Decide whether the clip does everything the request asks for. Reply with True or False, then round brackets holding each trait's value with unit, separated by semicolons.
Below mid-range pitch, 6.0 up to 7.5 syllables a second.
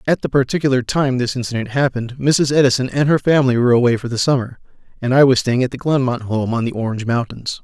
True (125 Hz; 6.7 syllables/s)